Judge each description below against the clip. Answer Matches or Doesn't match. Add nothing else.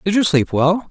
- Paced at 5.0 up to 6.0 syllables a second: Matches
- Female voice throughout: Doesn't match